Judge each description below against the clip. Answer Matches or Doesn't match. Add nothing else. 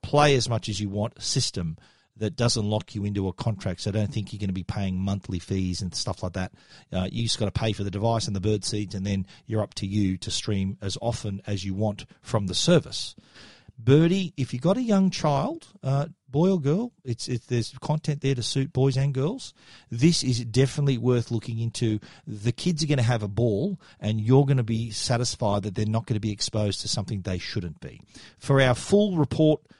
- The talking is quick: Matches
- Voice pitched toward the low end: Matches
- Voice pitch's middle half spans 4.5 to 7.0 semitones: Matches